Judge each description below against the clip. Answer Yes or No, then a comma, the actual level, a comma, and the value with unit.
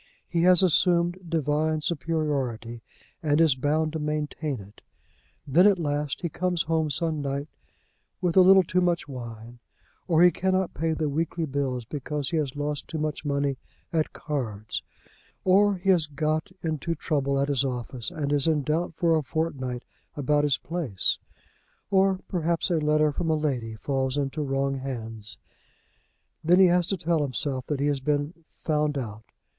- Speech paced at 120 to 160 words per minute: No, average, 170 wpm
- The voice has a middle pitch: Yes, medium, 150 Hz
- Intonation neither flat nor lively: Yes, average, 3.3 semitones